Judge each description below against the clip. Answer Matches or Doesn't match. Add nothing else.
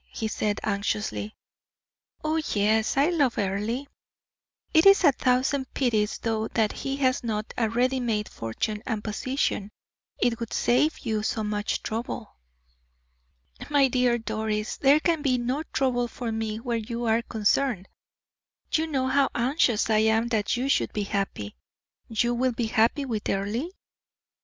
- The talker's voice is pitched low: Doesn't match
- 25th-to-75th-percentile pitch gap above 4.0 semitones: Doesn't match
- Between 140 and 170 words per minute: Matches